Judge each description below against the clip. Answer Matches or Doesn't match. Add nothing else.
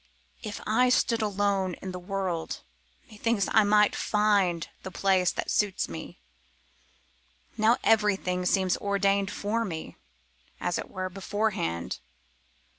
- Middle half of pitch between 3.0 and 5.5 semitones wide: Doesn't match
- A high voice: Matches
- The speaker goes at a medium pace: Doesn't match